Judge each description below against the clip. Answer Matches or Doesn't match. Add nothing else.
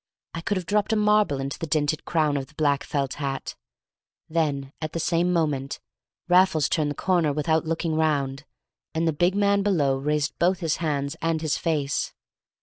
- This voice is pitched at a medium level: Matches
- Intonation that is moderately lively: Matches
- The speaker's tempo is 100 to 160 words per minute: Doesn't match